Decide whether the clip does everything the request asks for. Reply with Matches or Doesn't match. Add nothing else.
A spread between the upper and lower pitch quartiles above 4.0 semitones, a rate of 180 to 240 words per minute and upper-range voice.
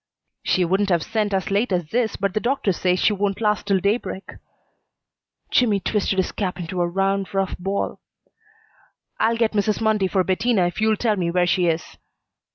Doesn't match